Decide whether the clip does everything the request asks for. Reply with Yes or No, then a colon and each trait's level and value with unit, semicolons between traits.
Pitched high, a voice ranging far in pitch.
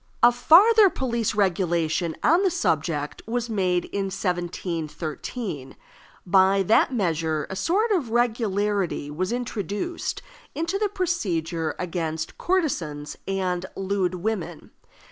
Yes: high, 195 Hz; wide, 6.3 semitones